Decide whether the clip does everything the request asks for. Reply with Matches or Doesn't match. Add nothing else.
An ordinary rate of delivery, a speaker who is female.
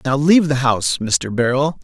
Doesn't match